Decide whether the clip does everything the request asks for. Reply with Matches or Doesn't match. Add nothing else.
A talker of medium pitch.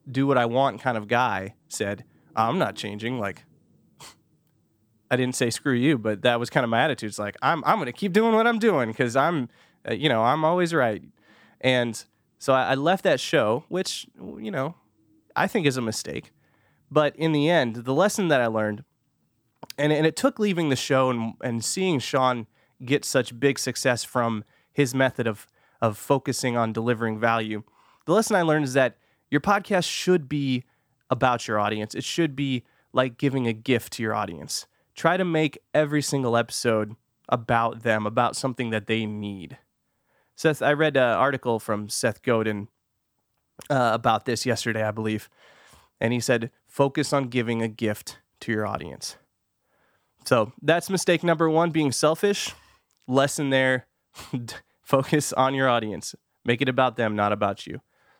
Doesn't match